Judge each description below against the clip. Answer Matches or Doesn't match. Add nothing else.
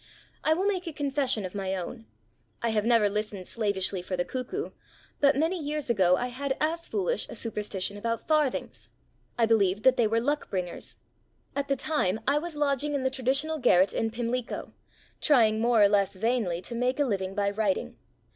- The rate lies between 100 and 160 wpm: Doesn't match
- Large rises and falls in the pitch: Matches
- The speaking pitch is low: Doesn't match